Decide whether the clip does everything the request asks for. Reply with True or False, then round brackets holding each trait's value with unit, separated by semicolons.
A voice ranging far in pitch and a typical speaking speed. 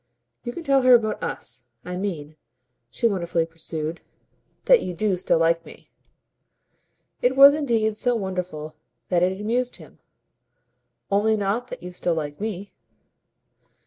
True (5.7 semitones; 145 wpm)